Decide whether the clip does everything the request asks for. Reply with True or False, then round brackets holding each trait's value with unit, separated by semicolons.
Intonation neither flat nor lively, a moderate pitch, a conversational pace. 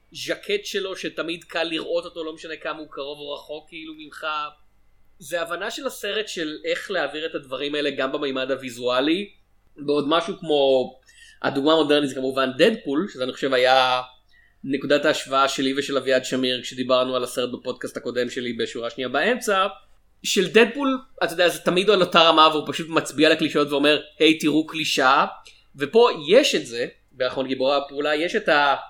False (4.5 semitones; 150 Hz; 170 wpm)